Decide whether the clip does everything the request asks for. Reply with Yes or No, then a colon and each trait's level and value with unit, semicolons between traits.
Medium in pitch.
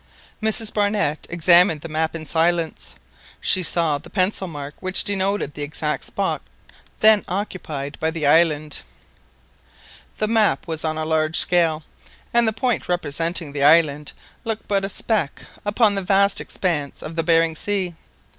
Yes: medium, 170 Hz